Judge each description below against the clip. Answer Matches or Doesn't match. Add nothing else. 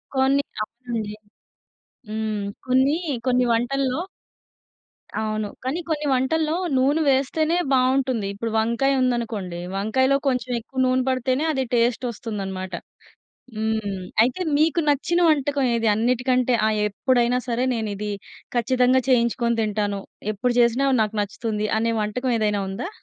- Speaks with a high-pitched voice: Matches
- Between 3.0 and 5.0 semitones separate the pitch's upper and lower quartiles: Matches